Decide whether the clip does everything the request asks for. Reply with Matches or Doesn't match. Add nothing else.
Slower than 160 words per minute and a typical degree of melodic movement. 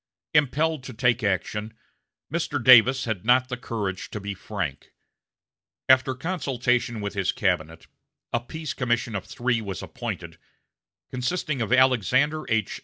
Matches